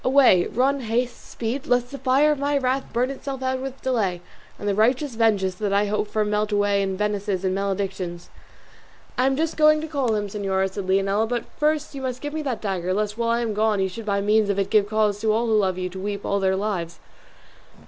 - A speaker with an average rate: No, fast, 235 wpm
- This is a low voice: No, high, 215 Hz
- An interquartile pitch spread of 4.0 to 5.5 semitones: Yes, average, 4.4 semitones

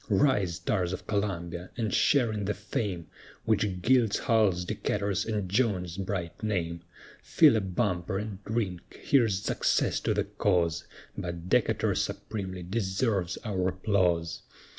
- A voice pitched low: Yes, very low, 95 Hz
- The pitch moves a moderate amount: Yes, average, 3.2 semitones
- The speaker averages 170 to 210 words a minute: No, slow, 135 wpm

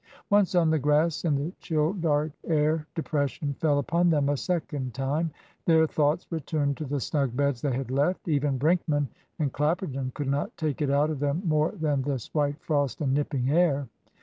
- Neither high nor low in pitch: Yes, medium, 150 Hz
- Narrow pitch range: Yes, narrow, 2.3 semitones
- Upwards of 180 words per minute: Yes, average, 190 wpm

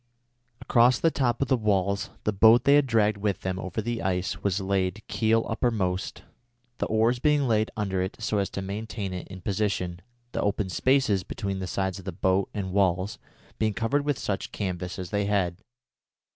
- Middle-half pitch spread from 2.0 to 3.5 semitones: Yes, average, 3.2 semitones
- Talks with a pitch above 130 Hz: No, low, 100 Hz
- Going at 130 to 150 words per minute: No, average, 195 wpm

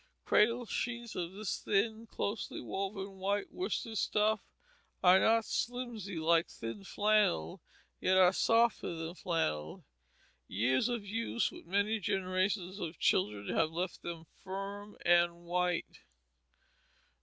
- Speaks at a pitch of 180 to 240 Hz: Yes, high, 190 Hz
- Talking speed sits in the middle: No, slow, 120 wpm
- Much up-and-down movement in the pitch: No, average, 3.9 semitones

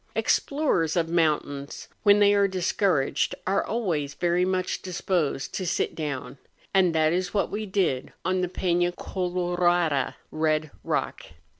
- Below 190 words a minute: Yes, average, 140 wpm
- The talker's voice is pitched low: No, medium, 175 Hz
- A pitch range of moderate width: Yes, average, 3.2 semitones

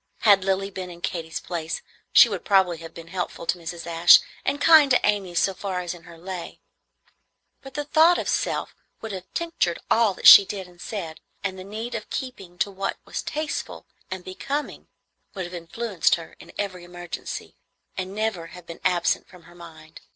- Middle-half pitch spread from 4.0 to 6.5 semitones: No, average, 3.2 semitones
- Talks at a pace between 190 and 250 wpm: Yes, average, 195 wpm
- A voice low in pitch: No, medium, 185 Hz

